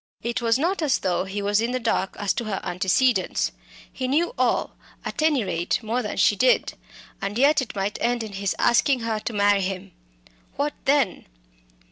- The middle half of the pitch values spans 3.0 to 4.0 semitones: No, average, 4.6 semitones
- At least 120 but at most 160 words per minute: No, average, 190 wpm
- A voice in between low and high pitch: No, high, 225 Hz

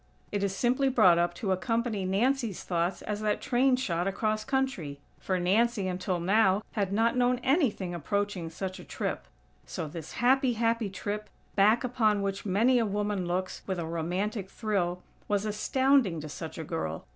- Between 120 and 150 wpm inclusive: No, average, 170 wpm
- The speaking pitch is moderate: No, high, 205 Hz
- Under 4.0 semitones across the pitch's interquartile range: No, average, 4.3 semitones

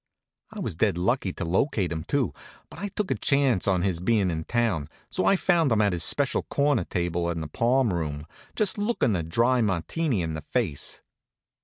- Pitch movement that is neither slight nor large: No, wide, 7.9 semitones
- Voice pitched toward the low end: Yes, low, 105 Hz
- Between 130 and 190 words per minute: No, average, 200 wpm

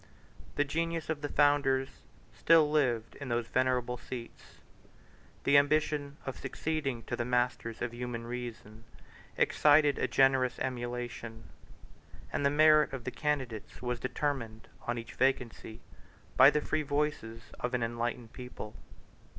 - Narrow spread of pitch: No, average, 3.4 semitones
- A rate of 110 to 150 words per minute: Yes, slow, 135 wpm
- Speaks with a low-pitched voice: Yes, low, 130 Hz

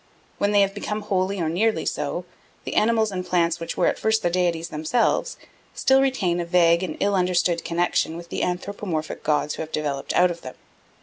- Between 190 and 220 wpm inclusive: Yes, average, 200 wpm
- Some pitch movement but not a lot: Yes, average, 3.2 semitones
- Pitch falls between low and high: Yes, medium, 180 Hz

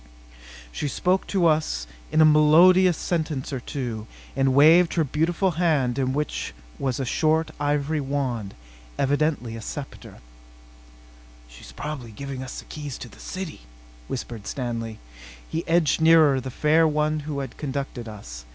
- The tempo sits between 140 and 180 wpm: Yes, average, 145 wpm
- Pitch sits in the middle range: Yes, medium, 145 Hz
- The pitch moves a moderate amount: Yes, average, 3.9 semitones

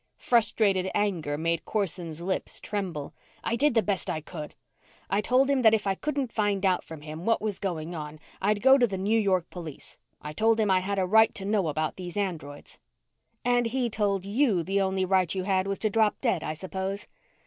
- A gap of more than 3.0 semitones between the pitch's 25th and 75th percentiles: Yes, average, 3.7 semitones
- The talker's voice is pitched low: No, high, 195 Hz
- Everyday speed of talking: No, fast, 210 wpm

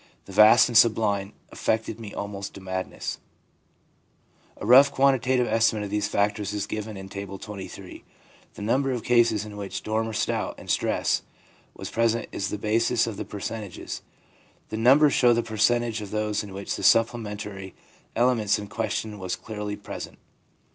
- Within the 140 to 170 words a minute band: Yes, average, 165 wpm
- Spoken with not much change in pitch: Yes, narrow, 2.3 semitones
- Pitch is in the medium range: No, low, 105 Hz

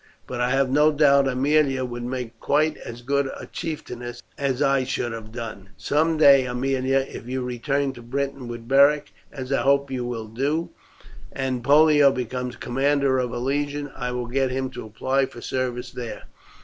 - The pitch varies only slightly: Yes, narrow, 2.3 semitones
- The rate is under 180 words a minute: No, average, 185 wpm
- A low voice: Yes, low, 130 Hz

